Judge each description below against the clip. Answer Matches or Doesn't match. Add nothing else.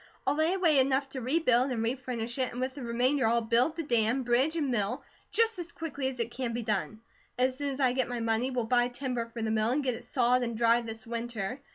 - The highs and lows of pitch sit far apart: Doesn't match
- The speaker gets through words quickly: Matches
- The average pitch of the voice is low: Doesn't match